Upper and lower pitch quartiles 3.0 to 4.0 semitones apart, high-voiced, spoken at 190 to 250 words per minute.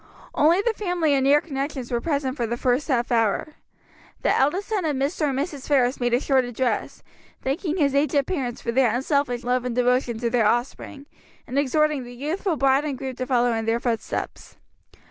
Yes: average, 3.3 semitones; very high, 265 Hz; average, 200 wpm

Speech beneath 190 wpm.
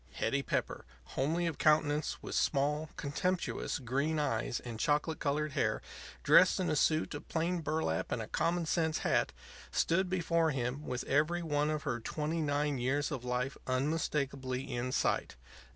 Yes: average, 160 wpm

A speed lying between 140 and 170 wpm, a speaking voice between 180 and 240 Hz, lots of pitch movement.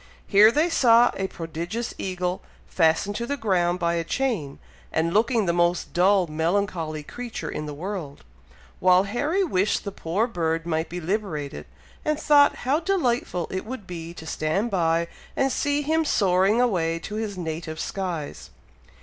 Yes: average, 160 wpm; medium, 185 Hz; wide, 5.9 semitones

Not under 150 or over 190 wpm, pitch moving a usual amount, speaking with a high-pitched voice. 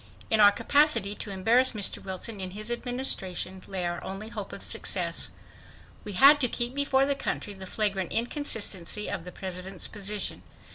Yes: average, 170 wpm; average, 4.3 semitones; high, 210 Hz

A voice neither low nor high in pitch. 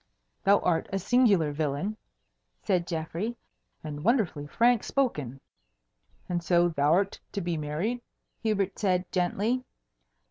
Yes: medium, 180 Hz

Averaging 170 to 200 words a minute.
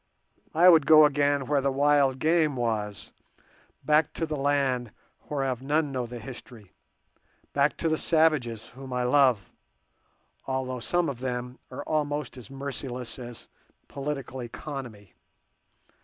No: slow, 135 wpm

